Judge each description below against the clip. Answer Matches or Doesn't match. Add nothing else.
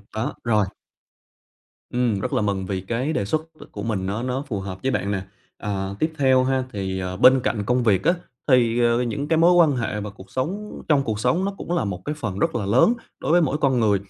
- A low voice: Matches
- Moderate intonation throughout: Doesn't match